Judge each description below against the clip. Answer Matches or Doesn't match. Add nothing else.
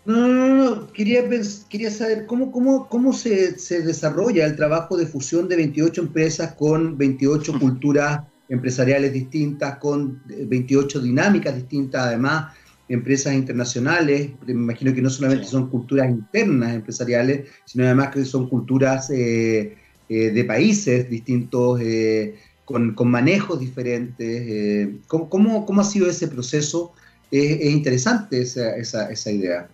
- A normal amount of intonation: Matches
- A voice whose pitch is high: Doesn't match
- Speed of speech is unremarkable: Matches